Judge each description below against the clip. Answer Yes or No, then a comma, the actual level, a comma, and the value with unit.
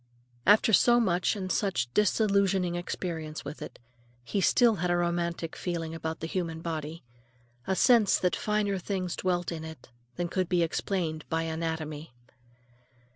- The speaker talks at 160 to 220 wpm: No, average, 150 wpm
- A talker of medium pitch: Yes, medium, 175 Hz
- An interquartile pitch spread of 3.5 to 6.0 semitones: No, average, 3.0 semitones